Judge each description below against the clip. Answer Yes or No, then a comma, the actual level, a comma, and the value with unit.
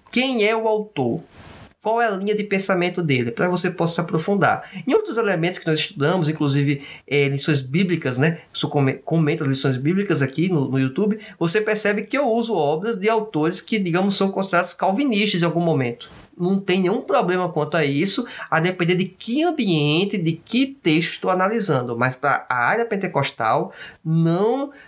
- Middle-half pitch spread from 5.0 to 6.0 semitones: Yes, wide, 5.5 semitones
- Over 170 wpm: Yes, average, 180 wpm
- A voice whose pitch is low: No, medium, 180 Hz